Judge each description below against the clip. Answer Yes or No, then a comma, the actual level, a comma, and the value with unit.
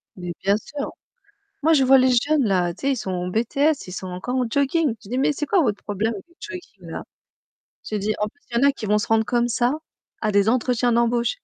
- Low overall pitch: No, high, 235 Hz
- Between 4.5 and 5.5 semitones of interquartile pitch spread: Yes, average, 4.9 semitones